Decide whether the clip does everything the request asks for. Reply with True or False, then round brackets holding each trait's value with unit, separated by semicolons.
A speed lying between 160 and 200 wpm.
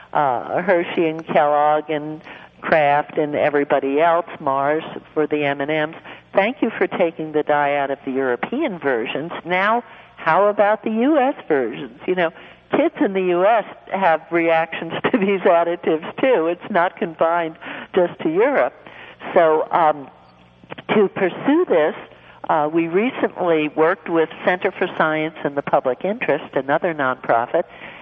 False (145 wpm)